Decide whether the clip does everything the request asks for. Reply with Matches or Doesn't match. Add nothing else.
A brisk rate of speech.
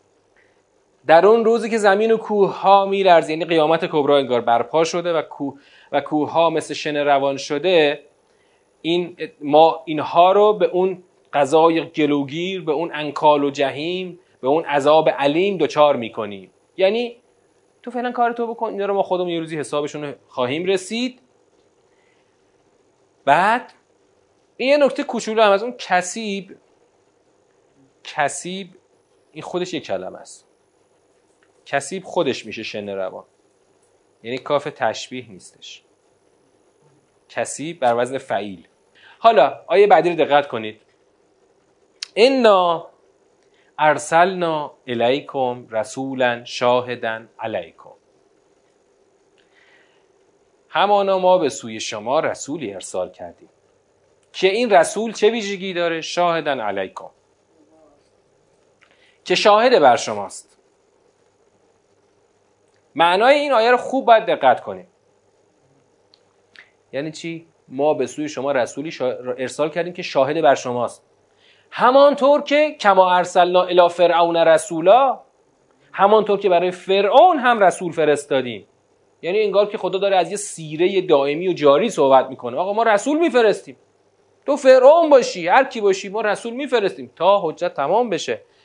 Doesn't match